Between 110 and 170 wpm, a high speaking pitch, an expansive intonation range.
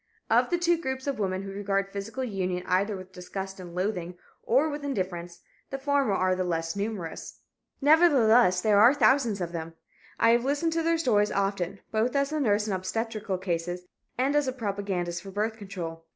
No: average, 195 wpm; high, 205 Hz; wide, 6.0 semitones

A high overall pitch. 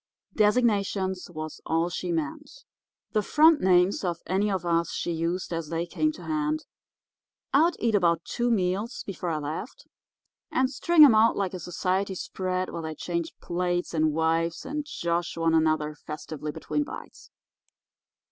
No: medium, 180 Hz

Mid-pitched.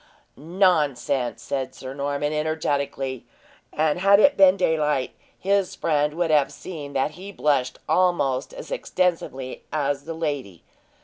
Yes: medium, 150 Hz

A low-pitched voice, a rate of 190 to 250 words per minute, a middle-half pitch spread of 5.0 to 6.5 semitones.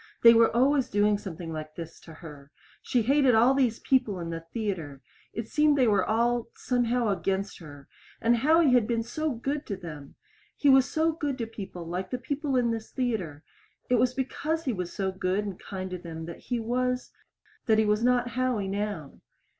No: high, 225 Hz; average, 200 wpm; wide, 5.4 semitones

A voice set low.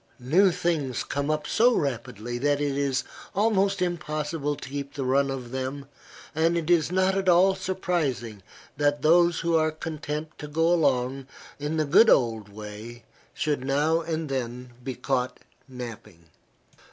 No: medium, 145 Hz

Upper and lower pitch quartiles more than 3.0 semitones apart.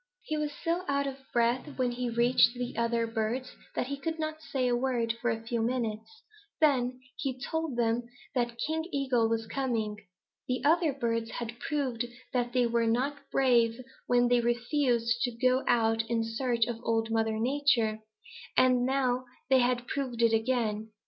No: narrow, 2.6 semitones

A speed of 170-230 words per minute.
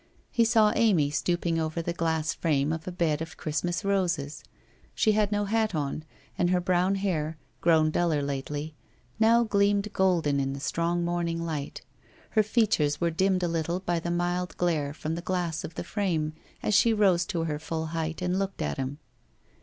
Yes: average, 185 wpm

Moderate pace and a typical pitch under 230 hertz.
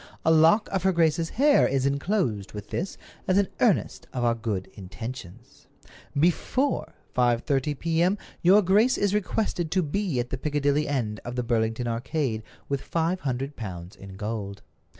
Yes: average, 160 wpm; medium, 140 Hz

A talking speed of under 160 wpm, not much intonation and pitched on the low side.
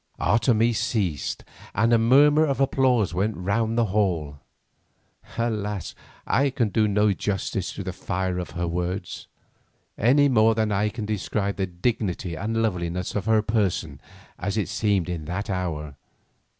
No: average, 150 wpm; average, 3.8 semitones; low, 105 Hz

